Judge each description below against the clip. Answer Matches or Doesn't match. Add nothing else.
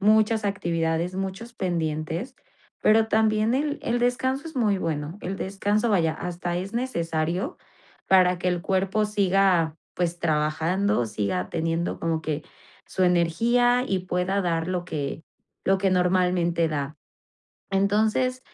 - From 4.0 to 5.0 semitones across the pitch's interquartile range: Matches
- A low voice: Doesn't match